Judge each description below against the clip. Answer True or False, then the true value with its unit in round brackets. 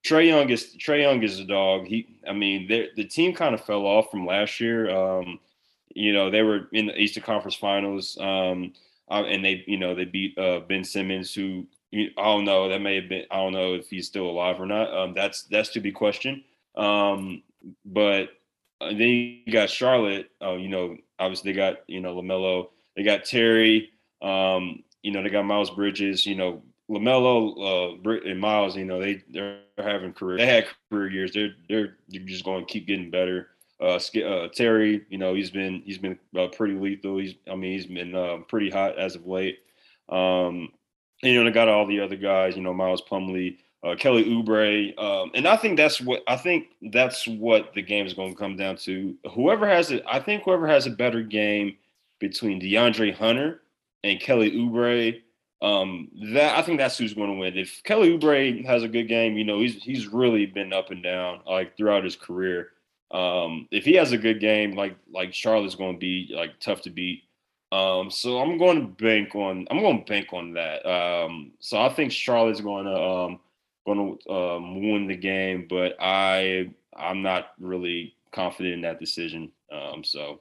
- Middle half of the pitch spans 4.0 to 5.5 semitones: False (2.9 semitones)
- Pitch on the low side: True (100 Hz)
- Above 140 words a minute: True (200 wpm)